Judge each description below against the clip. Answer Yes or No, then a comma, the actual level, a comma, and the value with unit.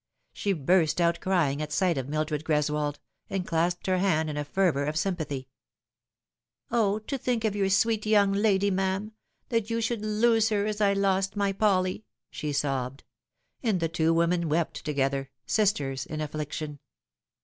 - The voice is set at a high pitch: No, medium, 180 Hz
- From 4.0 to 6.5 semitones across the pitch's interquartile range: Yes, average, 5.2 semitones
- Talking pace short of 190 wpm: Yes, average, 175 wpm